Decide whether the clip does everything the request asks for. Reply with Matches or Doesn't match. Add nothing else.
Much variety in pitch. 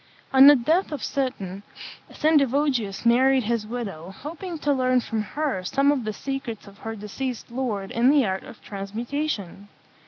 Doesn't match